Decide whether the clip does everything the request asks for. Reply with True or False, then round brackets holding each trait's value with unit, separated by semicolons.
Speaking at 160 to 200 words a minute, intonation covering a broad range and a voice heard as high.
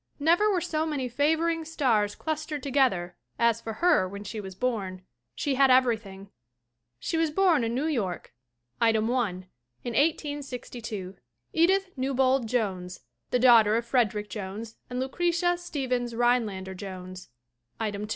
False (140 wpm; 6.0 semitones; 240 Hz)